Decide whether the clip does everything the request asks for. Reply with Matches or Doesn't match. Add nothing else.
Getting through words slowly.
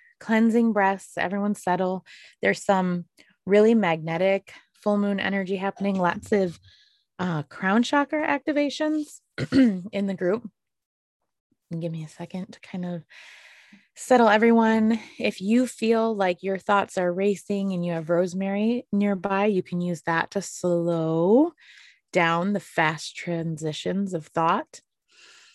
Matches